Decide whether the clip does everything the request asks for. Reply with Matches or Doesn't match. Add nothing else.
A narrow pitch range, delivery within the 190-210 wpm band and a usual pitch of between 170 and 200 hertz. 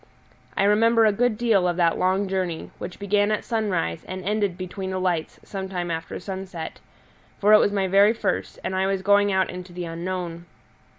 Matches